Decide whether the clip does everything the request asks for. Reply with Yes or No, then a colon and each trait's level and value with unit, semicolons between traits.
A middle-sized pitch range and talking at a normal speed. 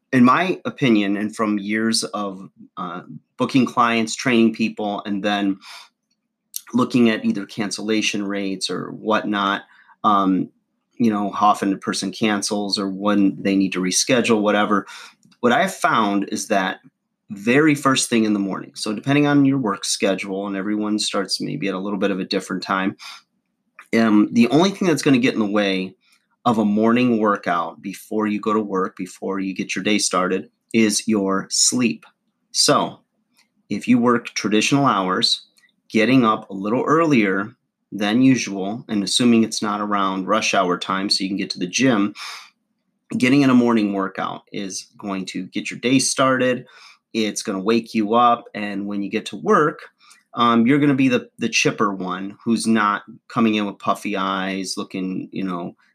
Yes: average, 3.5 semitones; average, 180 wpm